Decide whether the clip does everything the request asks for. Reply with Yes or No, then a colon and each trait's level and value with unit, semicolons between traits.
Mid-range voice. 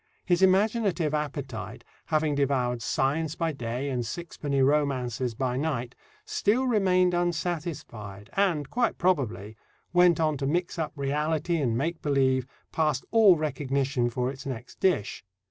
Yes: medium, 145 Hz